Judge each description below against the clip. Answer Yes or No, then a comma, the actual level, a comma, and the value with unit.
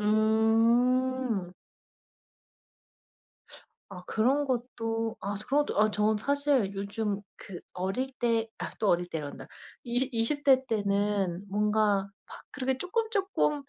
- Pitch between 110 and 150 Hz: No, high, 225 Hz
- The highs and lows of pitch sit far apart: No, average, 4.3 semitones